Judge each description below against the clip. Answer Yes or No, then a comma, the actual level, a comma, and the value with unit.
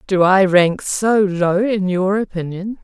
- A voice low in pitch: No, high, 190 Hz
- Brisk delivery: No, average, 170 wpm